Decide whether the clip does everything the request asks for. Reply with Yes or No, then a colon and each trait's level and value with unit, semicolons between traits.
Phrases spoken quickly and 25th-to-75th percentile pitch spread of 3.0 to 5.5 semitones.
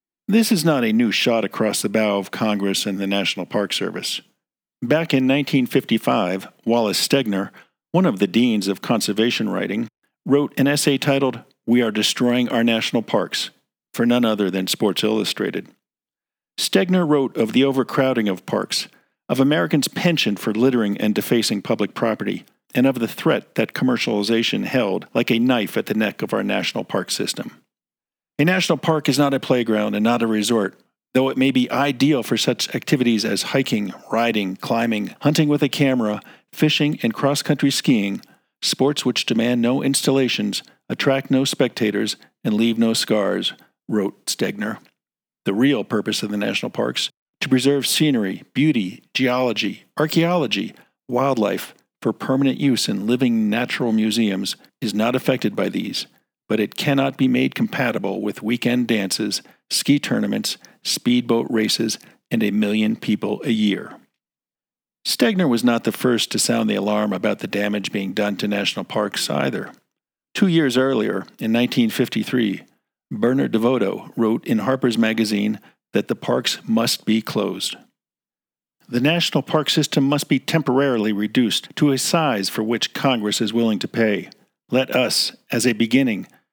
No: average, 155 wpm; average, 4.1 semitones